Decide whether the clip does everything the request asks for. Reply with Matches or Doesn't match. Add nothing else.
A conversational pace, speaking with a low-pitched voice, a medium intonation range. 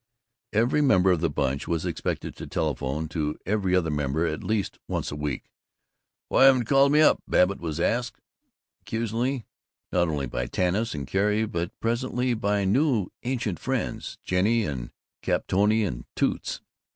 Doesn't match